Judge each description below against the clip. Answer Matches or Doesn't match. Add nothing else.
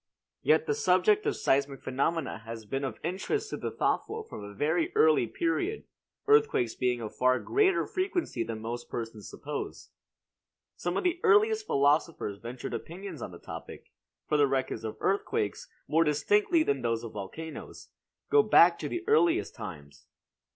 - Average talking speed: Matches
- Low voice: Doesn't match